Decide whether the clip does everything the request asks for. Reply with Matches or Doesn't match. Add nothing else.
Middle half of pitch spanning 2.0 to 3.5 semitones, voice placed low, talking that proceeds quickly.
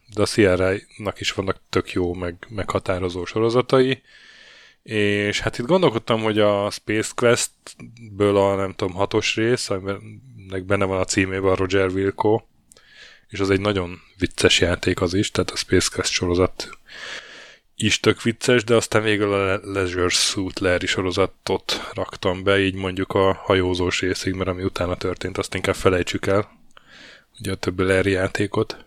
Matches